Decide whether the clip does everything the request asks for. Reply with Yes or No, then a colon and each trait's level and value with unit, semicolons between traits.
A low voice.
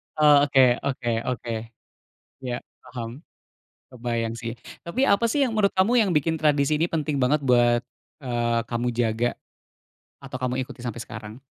Yes: low, 125 Hz